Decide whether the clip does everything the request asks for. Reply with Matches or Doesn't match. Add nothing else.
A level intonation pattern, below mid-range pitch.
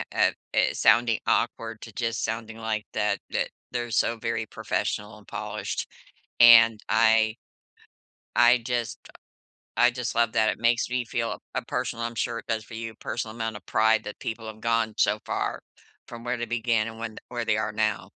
Matches